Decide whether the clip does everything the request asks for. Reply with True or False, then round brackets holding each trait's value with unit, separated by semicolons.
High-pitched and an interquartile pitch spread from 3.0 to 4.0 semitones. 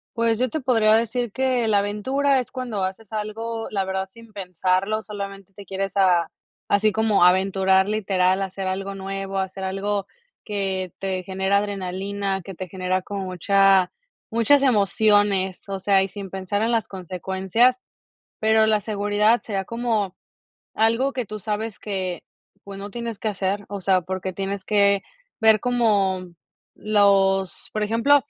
False (200 Hz; 2.4 semitones)